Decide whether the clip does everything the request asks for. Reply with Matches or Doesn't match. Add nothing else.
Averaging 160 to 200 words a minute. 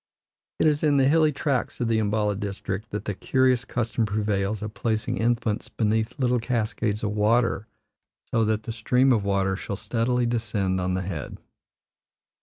Matches